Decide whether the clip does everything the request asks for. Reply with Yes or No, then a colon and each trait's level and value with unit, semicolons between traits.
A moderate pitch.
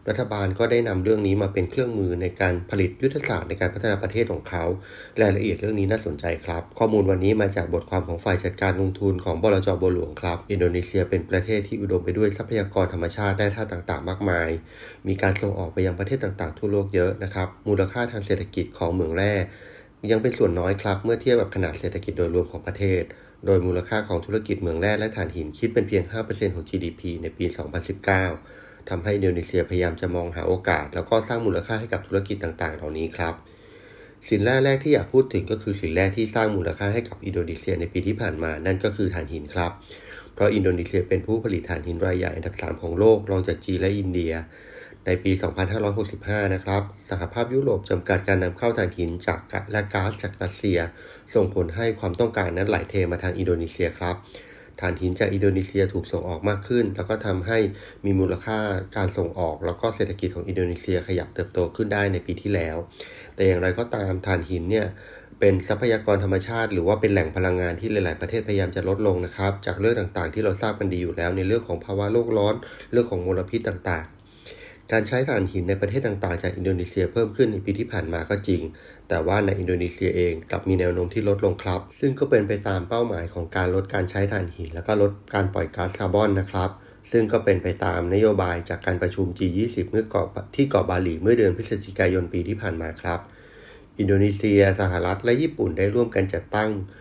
No: very low, 95 Hz